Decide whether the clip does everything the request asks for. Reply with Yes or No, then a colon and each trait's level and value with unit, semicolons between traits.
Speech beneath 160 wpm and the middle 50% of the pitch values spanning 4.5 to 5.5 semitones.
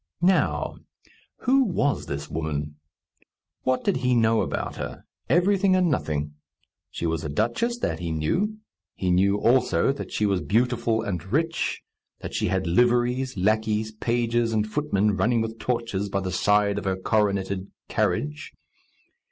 Yes: average, 150 wpm; average, 5.0 semitones